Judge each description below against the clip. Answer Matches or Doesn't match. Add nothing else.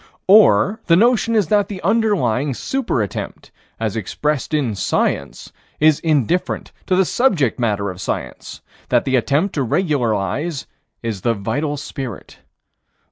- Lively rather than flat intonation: Matches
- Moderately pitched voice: Matches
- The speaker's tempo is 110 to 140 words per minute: Matches